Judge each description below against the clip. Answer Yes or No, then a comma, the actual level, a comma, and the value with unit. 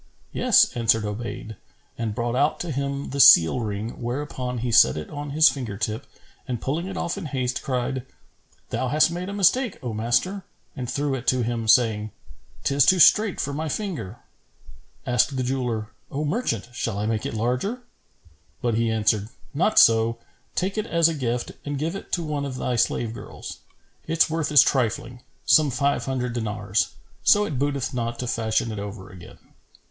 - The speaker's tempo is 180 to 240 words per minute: Yes, average, 185 wpm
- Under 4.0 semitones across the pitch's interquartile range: No, average, 4.6 semitones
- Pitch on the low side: Yes, low, 125 Hz